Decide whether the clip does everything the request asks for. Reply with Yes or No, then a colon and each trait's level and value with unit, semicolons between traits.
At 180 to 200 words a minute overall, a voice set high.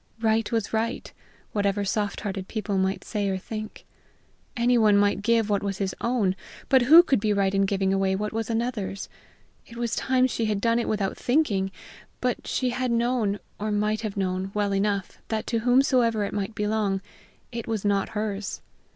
Yes: average, 185 wpm; high, 210 Hz